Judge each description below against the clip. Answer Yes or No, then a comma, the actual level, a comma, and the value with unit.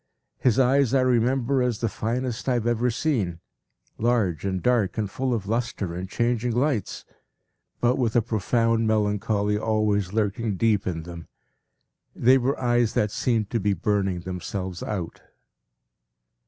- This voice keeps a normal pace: Yes, average, 150 wpm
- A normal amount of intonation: Yes, average, 3.4 semitones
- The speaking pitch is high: No, low, 110 Hz